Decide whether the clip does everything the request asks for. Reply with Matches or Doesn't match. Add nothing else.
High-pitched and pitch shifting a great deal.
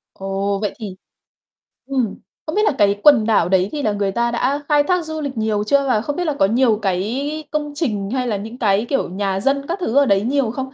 Matches